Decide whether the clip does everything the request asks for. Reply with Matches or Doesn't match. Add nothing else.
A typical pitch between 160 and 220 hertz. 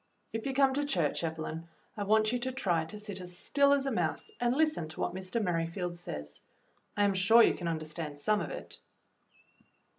Matches